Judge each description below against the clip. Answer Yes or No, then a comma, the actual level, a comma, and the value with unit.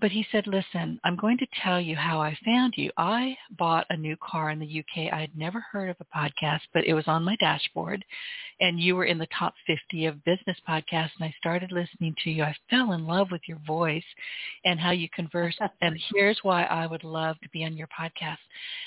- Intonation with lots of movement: No, average, 3.7 semitones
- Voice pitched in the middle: Yes, medium, 170 Hz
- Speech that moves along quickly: Yes, fast, 230 wpm